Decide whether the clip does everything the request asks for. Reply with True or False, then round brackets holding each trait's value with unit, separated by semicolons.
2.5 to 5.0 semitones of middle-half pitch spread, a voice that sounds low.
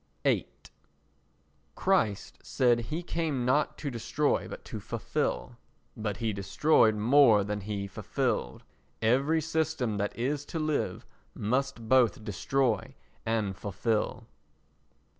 False (5.5 semitones; 120 Hz)